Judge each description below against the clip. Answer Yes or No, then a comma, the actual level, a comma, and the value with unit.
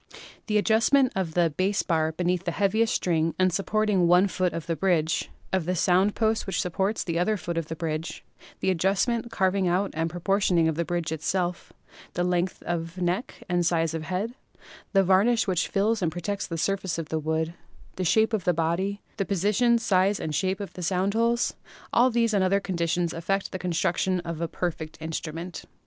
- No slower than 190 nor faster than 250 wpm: Yes, average, 200 wpm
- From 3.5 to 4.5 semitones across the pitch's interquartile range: No, average, 3.1 semitones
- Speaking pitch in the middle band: Yes, medium, 180 Hz